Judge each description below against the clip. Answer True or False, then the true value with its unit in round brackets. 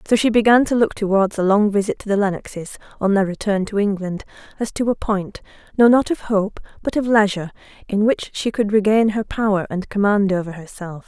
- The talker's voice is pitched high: True (205 Hz)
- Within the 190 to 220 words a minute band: True (200 wpm)